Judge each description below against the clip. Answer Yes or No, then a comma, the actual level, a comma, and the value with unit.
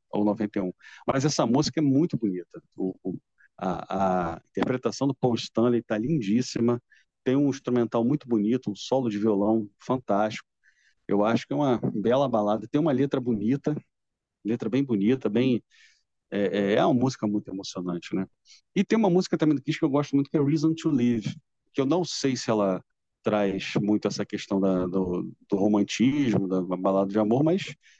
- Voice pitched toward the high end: No, low, 115 Hz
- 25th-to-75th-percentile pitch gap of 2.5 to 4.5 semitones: No, average, 5.2 semitones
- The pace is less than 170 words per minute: No, average, 180 wpm